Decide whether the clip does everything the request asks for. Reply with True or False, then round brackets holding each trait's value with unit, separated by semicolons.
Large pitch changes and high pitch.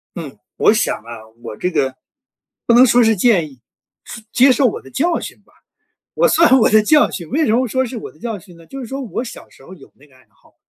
True (7.8 semitones; 220 Hz)